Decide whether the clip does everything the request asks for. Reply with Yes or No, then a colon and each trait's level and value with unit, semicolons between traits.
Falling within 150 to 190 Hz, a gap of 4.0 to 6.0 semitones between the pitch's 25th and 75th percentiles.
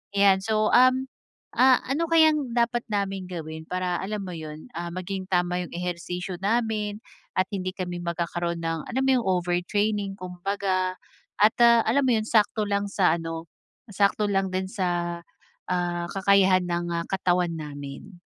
No: medium, 185 Hz; average, 3.1 semitones